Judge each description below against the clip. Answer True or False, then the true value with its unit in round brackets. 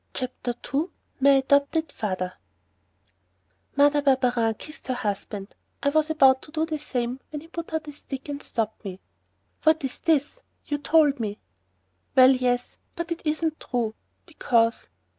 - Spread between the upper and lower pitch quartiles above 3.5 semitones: True (4.0 semitones)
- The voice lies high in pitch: True (275 Hz)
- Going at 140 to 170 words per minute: True (150 wpm)